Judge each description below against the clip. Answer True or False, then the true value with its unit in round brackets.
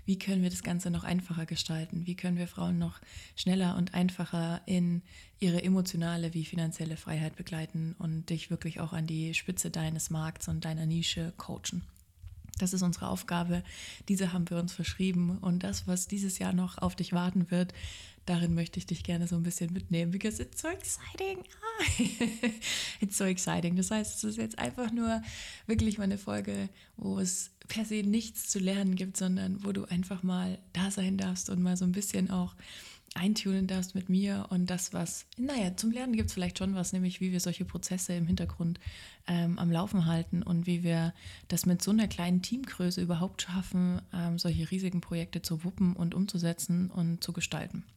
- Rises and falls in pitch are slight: True (1.9 semitones)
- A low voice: False (180 Hz)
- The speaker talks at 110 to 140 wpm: False (190 wpm)